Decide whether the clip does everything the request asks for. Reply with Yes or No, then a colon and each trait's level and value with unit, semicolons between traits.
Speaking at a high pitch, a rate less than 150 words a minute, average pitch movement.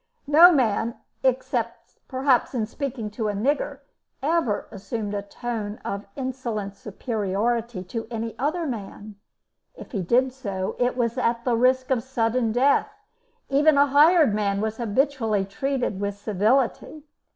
Yes: high, 235 Hz; average, 140 wpm; average, 4.0 semitones